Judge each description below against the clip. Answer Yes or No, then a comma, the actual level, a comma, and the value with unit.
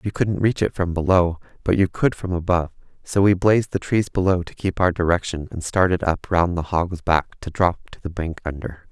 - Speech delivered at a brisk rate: Yes, fast, 230 wpm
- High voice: No, very low, 90 Hz